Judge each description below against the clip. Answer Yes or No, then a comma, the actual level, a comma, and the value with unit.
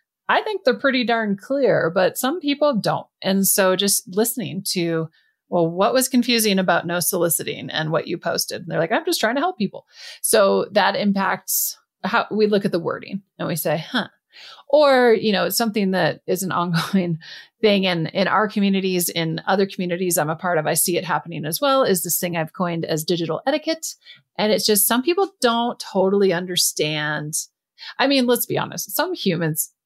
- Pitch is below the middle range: No, high, 190 Hz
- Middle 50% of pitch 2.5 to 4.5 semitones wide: No, wide, 5.4 semitones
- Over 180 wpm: Yes, average, 200 wpm